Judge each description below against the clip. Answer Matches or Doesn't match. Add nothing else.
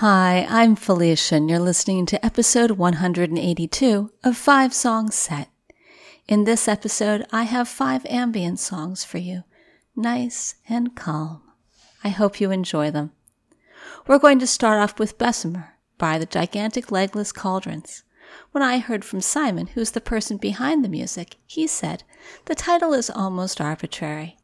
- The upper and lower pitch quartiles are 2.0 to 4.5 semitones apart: Doesn't match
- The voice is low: Doesn't match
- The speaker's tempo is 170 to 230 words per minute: Doesn't match